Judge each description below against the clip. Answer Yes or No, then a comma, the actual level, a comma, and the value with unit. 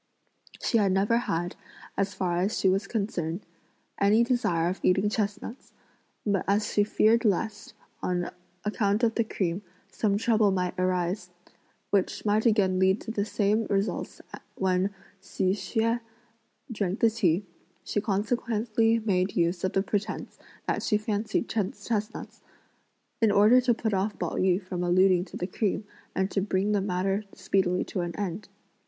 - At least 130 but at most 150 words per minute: No, average, 160 wpm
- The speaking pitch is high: Yes, high, 200 Hz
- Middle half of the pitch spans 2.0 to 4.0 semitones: Yes, narrow, 2.6 semitones